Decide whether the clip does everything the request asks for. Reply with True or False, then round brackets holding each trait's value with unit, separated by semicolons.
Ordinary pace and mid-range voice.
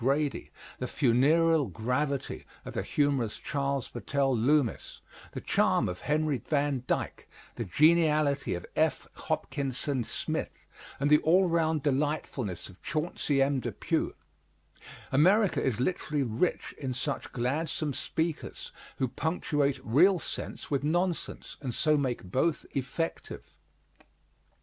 False (120 wpm; 145 Hz)